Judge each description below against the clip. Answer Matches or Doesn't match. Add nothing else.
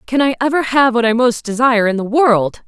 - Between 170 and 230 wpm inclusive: Doesn't match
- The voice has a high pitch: Matches